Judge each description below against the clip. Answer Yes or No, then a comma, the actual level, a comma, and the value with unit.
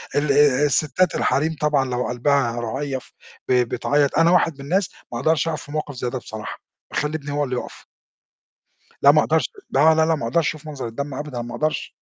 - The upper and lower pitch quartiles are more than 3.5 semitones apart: No, average, 3.2 semitones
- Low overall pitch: No, medium, 145 Hz